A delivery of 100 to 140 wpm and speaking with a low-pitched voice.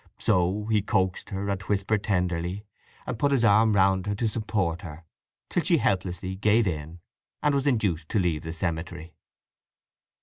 No: average, 165 wpm; very low, 95 Hz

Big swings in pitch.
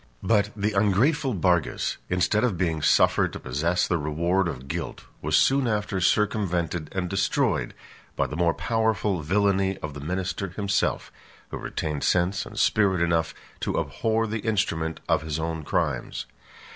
No: average, 4.3 semitones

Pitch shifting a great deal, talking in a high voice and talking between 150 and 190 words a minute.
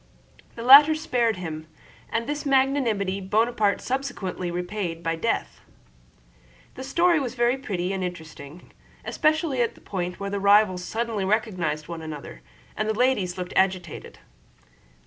No: wide, 5.8 semitones; high, 205 Hz; average, 140 wpm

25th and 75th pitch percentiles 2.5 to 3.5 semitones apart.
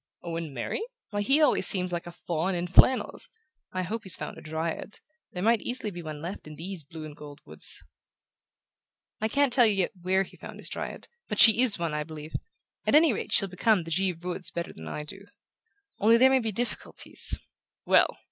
No: average, 5.1 semitones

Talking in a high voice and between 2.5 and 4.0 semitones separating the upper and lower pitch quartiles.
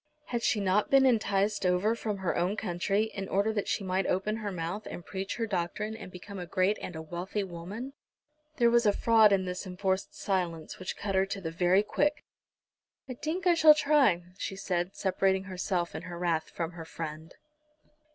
Yes: high, 195 Hz; average, 3.1 semitones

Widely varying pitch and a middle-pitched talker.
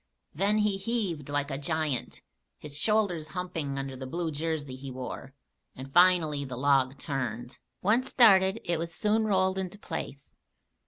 Yes: wide, 5.7 semitones; medium, 160 Hz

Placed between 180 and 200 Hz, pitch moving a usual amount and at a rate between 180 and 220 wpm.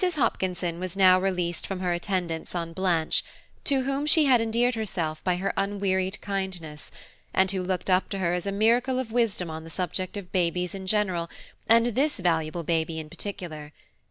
Yes: medium, 185 Hz; average, 3.4 semitones; average, 185 wpm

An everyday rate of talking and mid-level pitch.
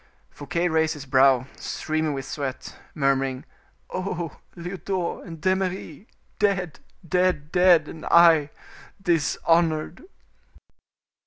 No: slow, 95 wpm; medium, 165 Hz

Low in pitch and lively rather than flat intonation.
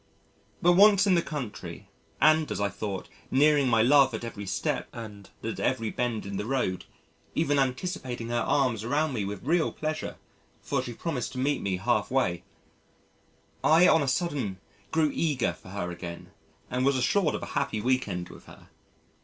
Yes: low, 125 Hz; wide, 6.2 semitones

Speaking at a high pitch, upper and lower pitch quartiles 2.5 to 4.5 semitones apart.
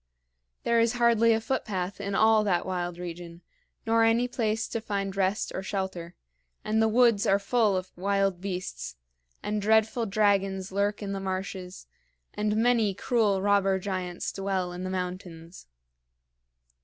Yes: high, 200 Hz; average, 2.9 semitones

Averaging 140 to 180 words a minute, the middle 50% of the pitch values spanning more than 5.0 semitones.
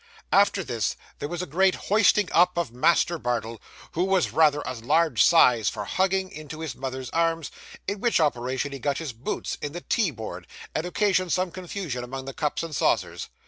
No: average, 190 wpm; wide, 5.4 semitones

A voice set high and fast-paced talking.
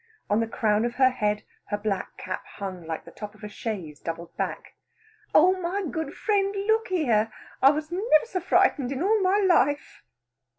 No: very high, 265 Hz; average, 185 wpm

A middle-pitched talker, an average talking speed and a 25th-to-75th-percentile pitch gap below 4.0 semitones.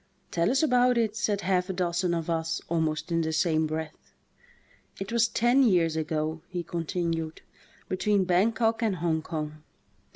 No: medium, 175 Hz; average, 160 wpm; average, 4.6 semitones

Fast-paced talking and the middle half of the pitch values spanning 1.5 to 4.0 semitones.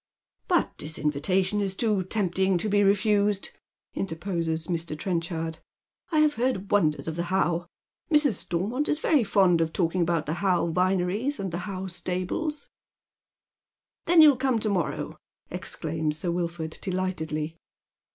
No: average, 145 wpm; average, 3.7 semitones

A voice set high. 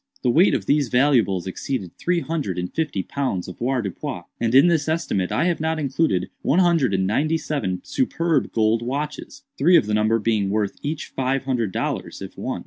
No: low, 130 Hz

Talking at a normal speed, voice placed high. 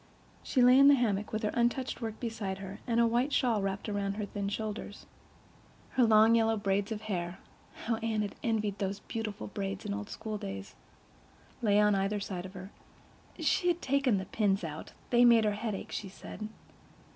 Yes: average, 180 wpm; high, 210 Hz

